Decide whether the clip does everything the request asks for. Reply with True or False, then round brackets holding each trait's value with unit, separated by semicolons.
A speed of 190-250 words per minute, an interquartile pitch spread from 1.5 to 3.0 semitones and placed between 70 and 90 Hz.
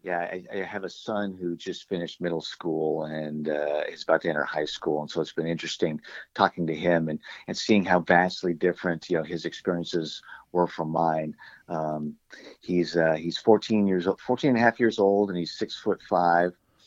True (205 wpm; 2.6 semitones; 85 Hz)